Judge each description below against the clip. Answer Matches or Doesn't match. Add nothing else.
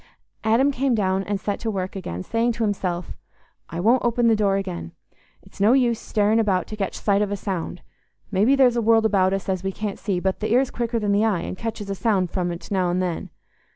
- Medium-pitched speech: Doesn't match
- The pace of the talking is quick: Matches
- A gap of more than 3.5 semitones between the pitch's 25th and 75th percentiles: Doesn't match